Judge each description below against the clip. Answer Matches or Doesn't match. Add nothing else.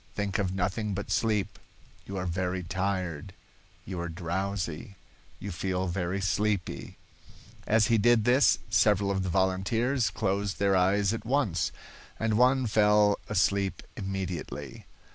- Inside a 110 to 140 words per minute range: Matches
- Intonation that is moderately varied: Doesn't match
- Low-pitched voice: Matches